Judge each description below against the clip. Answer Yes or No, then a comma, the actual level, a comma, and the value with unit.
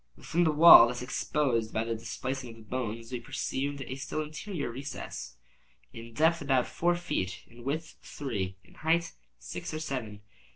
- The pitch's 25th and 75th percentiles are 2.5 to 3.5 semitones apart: No, average, 5.1 semitones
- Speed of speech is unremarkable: Yes, average, 170 wpm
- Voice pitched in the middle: No, low, 130 Hz